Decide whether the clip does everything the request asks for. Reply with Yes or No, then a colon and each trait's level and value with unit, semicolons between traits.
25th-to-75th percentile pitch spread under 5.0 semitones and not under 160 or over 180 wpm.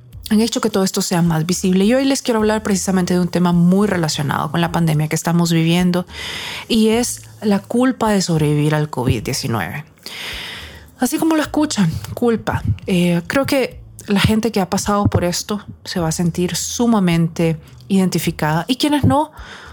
No: wide, 5.4 semitones; average, 175 wpm